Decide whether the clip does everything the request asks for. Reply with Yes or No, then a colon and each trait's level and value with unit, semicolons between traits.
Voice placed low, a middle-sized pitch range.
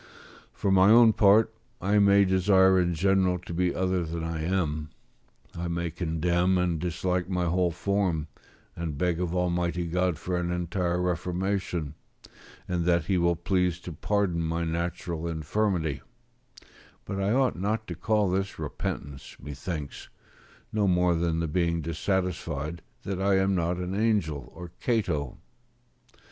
No: very low, 90 Hz; narrow, 2.2 semitones